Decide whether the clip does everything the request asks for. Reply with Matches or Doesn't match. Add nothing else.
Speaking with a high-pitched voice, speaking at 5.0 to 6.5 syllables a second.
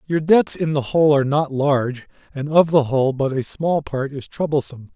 Doesn't match